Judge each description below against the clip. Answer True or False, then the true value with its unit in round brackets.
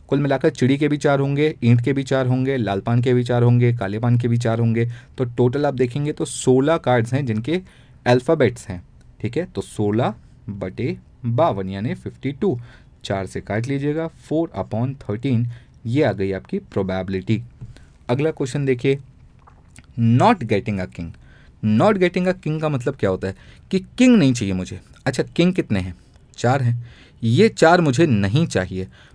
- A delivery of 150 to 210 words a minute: True (165 wpm)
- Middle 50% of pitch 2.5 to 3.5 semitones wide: False (4.9 semitones)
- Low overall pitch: True (125 Hz)